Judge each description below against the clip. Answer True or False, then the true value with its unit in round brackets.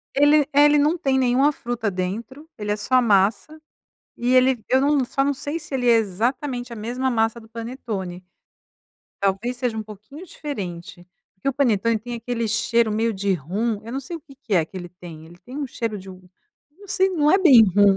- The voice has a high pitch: True (235 Hz)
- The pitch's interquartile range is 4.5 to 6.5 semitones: True (5.0 semitones)